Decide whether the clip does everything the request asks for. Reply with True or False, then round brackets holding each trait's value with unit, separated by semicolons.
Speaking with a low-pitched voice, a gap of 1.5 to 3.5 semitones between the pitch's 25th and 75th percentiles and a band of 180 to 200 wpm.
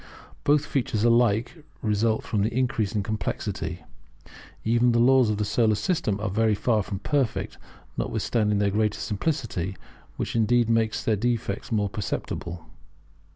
False (110 Hz; 2.5 semitones; 145 wpm)